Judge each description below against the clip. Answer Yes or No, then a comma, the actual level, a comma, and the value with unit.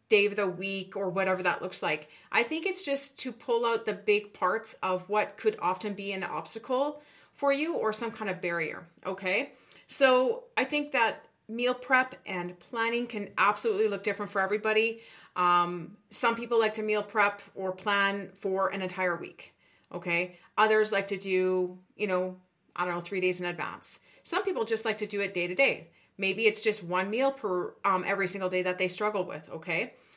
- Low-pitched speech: No, high, 205 Hz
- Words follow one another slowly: No, average, 200 wpm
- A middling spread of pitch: Yes, average, 3.7 semitones